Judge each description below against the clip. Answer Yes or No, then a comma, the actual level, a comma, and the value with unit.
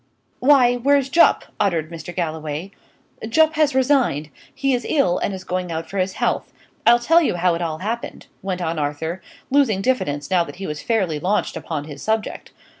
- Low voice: No, high, 190 Hz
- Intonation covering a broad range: Yes, wide, 7.4 semitones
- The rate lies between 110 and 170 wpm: No, average, 190 wpm